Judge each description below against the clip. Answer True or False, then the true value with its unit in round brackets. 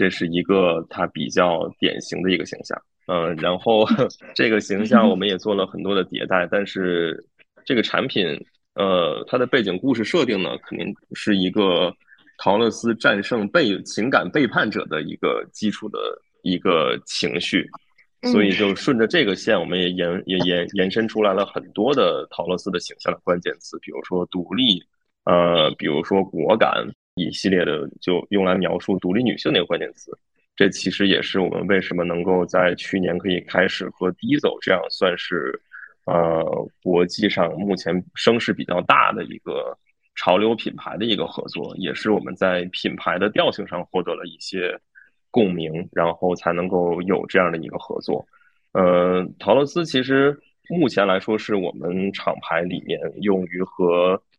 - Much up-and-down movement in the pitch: False (2.1 semitones)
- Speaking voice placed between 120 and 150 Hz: False (95 Hz)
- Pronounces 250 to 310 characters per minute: True (260 characters per minute)